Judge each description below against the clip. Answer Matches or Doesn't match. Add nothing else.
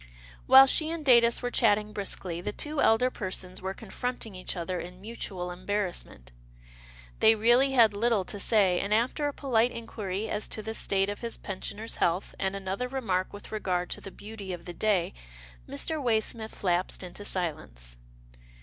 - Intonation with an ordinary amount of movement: Matches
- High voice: Matches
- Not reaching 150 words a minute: Doesn't match